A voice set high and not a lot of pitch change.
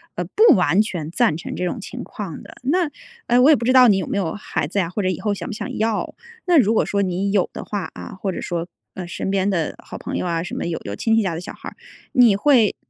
No: high, 200 Hz; average, 4.4 semitones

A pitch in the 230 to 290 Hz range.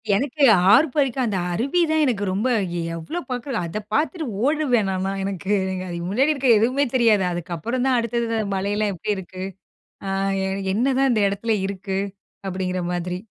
No: high, 215 Hz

